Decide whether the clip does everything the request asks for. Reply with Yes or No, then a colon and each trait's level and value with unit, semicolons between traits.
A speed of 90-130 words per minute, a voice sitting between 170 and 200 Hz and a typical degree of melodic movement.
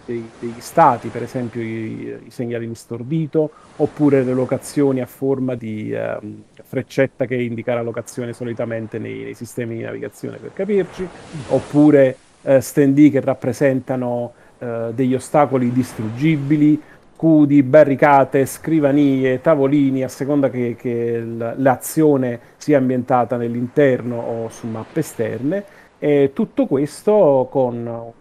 No: average, 125 wpm; low, 130 Hz; average, 3.4 semitones